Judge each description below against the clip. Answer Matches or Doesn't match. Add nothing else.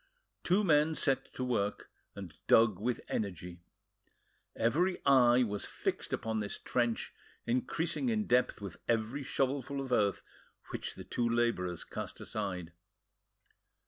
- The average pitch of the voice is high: Doesn't match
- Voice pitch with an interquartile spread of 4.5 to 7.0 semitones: Matches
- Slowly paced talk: Matches